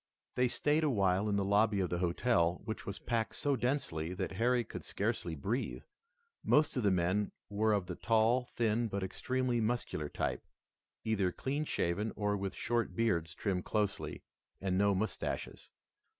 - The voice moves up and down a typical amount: Yes, average, 4.2 semitones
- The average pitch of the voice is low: Yes, low, 105 Hz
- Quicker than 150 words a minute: Yes, average, 165 wpm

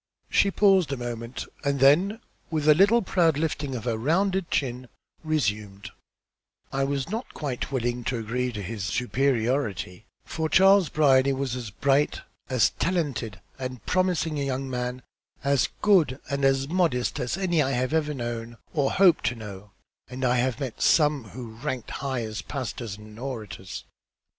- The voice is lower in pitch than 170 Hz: Yes, low, 135 Hz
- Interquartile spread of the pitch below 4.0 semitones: No, average, 4.3 semitones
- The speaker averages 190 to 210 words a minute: No, average, 160 wpm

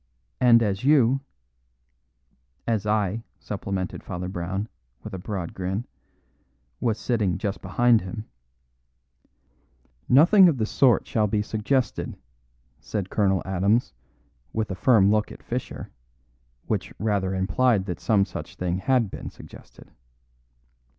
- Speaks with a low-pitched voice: Yes, low, 100 Hz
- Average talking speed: No, slow, 130 wpm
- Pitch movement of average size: Yes, average, 3.7 semitones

